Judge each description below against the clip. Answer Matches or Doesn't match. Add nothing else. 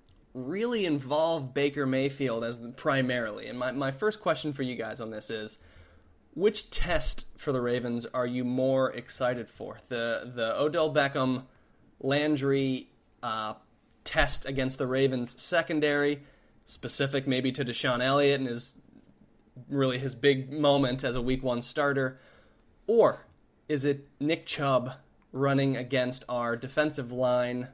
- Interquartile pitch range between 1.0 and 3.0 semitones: Matches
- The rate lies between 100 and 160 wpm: Matches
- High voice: Doesn't match